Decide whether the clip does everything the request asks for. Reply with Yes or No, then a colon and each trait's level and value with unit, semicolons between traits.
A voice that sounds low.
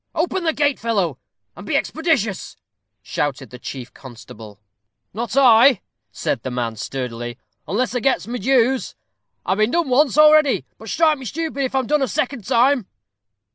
No: high, 240 Hz